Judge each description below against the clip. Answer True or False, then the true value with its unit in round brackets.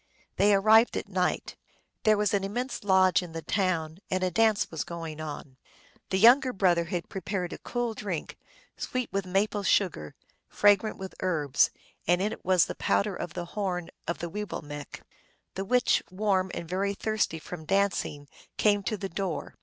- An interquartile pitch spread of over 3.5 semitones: False (3.2 semitones)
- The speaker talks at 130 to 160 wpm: False (175 wpm)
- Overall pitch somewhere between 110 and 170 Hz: False (190 Hz)